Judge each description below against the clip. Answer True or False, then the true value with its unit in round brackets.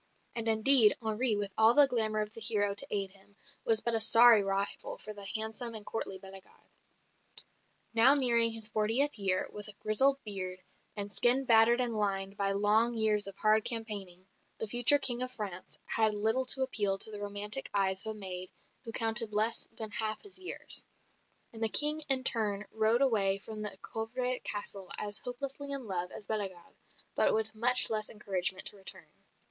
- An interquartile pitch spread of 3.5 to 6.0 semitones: False (2.6 semitones)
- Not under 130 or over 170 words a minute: False (185 wpm)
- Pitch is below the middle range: False (215 Hz)